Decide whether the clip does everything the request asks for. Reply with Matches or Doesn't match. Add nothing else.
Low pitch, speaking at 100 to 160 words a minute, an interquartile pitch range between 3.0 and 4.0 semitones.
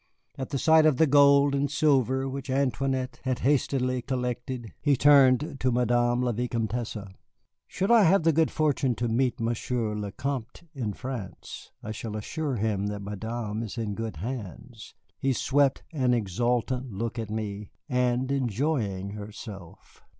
Matches